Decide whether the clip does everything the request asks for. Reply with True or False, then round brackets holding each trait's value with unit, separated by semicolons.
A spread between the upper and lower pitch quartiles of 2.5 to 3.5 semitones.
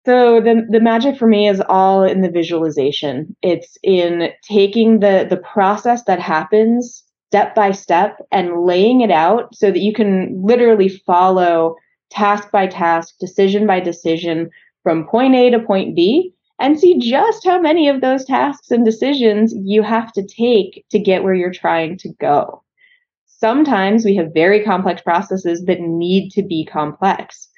False (4.5 semitones)